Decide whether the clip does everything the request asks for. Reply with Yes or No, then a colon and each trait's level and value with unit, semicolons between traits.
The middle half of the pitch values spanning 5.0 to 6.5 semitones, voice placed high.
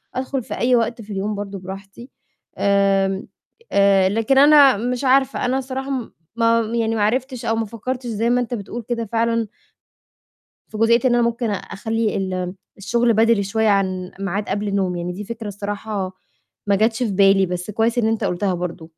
No: average, 3.1 semitones; high, 220 Hz